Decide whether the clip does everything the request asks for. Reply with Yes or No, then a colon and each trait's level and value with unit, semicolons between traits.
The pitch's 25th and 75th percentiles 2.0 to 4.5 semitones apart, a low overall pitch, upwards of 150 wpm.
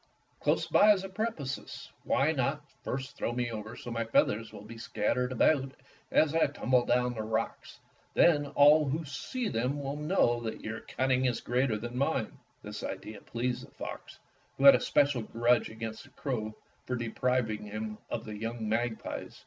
Yes: average, 3.7 semitones; low, 125 Hz; average, 180 wpm